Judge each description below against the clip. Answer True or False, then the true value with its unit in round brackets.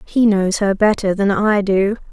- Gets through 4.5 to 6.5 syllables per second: False (4.2 syllables/s)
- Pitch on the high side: True (200 Hz)